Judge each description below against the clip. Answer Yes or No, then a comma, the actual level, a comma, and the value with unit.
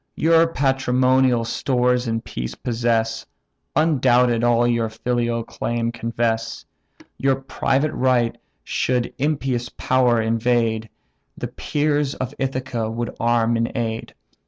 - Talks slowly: Yes, slow, 110 wpm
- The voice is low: Yes, low, 120 Hz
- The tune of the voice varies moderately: No, narrow, 2.2 semitones